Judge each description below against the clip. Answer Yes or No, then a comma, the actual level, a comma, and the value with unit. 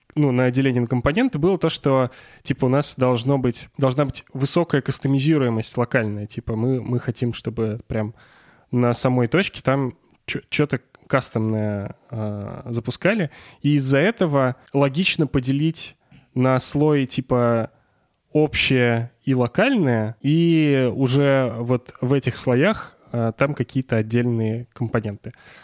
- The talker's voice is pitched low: Yes, low, 130 Hz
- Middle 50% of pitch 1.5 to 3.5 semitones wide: Yes, average, 3.0 semitones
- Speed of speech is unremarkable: Yes, average, 125 wpm